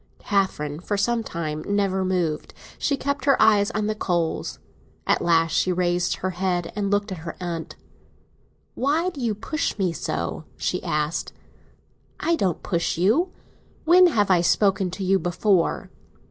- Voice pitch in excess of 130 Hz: Yes, high, 190 Hz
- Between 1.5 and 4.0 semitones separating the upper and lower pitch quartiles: Yes, average, 3.6 semitones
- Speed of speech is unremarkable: Yes, average, 160 wpm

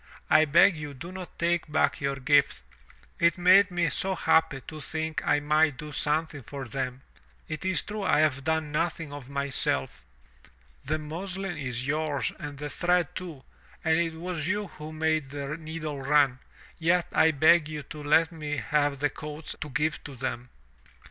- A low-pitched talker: No, medium, 155 Hz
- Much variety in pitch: No, average, 2.7 semitones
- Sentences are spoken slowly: No, average, 175 wpm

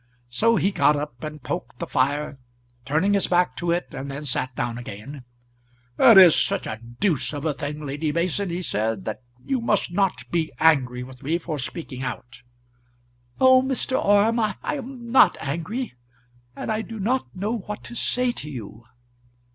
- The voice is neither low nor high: Yes, medium, 160 Hz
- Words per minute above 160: Yes, average, 180 wpm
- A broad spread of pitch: Yes, wide, 7.6 semitones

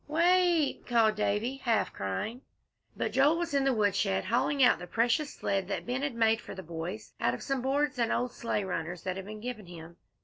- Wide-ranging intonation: Yes, wide, 5.9 semitones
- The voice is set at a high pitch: Yes, high, 230 Hz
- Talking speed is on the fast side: Yes, fast, 215 wpm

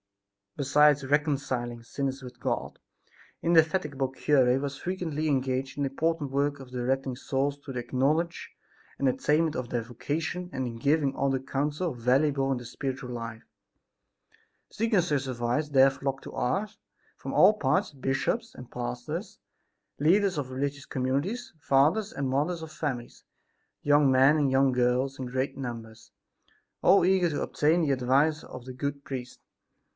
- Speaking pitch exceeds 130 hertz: Yes, medium, 140 Hz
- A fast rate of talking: No, average, 150 wpm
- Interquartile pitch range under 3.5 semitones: Yes, average, 2.9 semitones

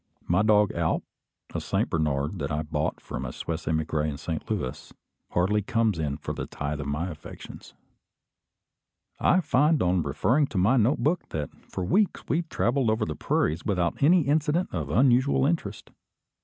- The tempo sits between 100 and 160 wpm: No, average, 170 wpm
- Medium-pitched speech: No, very low, 95 Hz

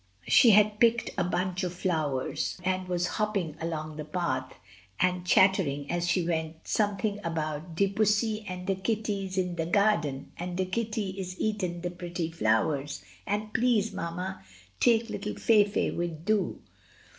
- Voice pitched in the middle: Yes, medium, 180 Hz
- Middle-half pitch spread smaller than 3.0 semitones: No, average, 3.9 semitones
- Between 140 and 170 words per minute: Yes, average, 155 wpm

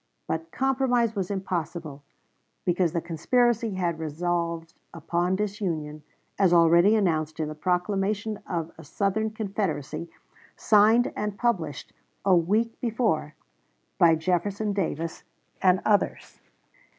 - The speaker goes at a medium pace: No, slow, 115 wpm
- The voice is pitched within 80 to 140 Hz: No, medium, 180 Hz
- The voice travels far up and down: No, average, 4.3 semitones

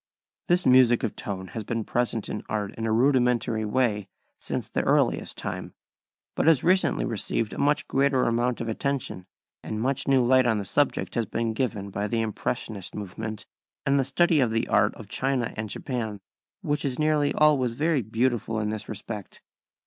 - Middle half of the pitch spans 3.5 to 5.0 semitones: Yes, average, 3.9 semitones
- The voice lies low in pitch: Yes, low, 120 Hz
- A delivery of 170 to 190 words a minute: Yes, average, 180 wpm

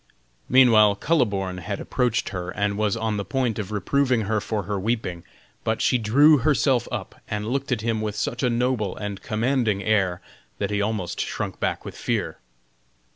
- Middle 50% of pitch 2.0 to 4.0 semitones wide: Yes, average, 3.4 semitones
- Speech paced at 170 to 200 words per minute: Yes, average, 180 wpm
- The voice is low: Yes, low, 110 Hz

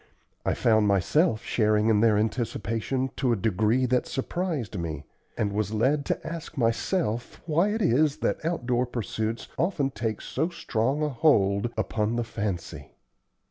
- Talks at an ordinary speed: Yes, average, 150 wpm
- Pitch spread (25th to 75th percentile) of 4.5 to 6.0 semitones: Yes, average, 5.1 semitones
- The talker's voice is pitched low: Yes, low, 115 Hz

